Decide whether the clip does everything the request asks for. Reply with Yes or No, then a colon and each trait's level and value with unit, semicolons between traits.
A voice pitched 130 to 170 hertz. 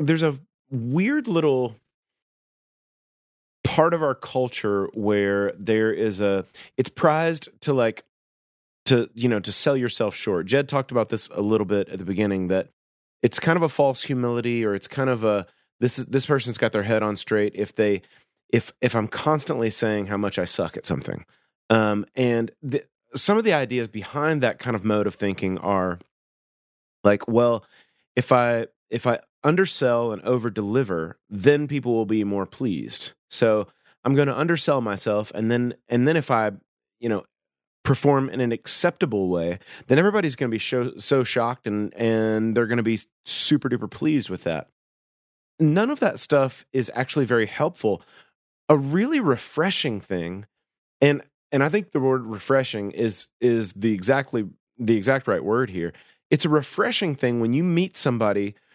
No: low, 120 Hz